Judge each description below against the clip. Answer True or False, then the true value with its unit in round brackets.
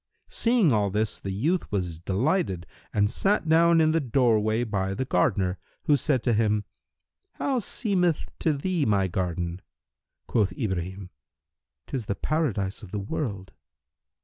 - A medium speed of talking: True (145 wpm)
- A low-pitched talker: True (110 Hz)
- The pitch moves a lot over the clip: True (8.4 semitones)